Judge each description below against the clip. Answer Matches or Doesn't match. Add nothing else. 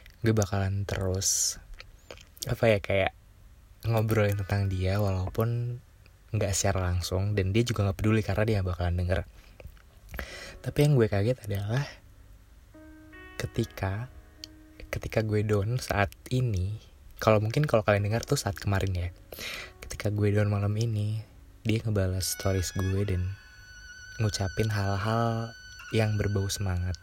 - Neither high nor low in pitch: Doesn't match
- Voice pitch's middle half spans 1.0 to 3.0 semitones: Matches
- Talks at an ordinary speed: Matches